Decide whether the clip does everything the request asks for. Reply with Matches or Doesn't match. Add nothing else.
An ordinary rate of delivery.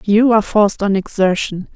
Matches